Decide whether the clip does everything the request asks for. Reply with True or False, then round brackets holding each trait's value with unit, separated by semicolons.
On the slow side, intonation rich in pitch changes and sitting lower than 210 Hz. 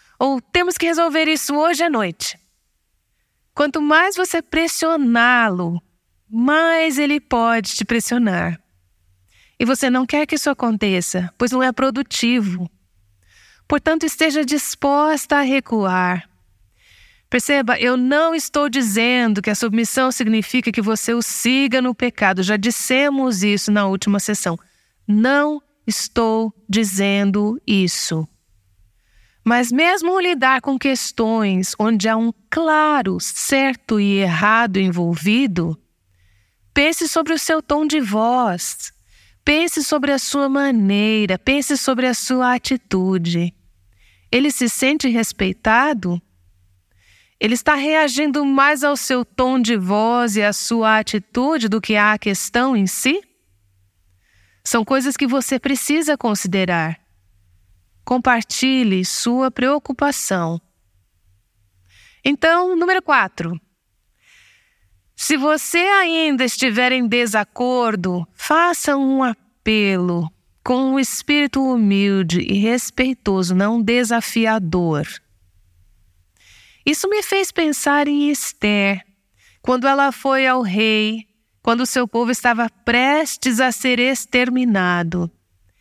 False (110 wpm; 6.8 semitones; 235 Hz)